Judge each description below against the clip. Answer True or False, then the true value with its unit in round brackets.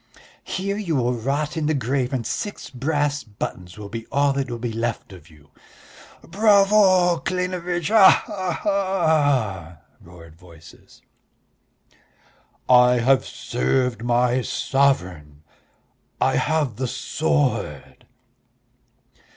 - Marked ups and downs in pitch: True (6.9 semitones)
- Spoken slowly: True (110 wpm)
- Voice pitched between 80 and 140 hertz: True (135 Hz)